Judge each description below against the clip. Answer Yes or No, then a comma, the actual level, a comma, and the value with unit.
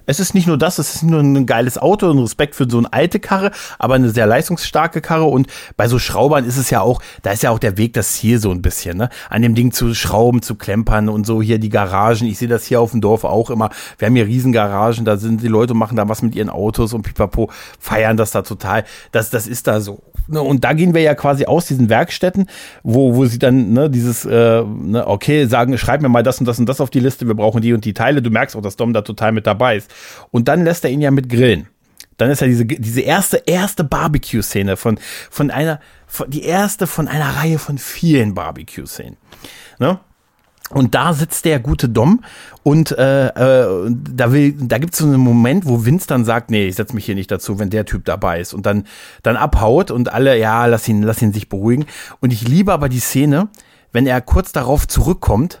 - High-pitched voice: No, low, 120 Hz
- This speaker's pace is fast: Yes, fast, 235 wpm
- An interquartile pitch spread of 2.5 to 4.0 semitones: No, average, 4.5 semitones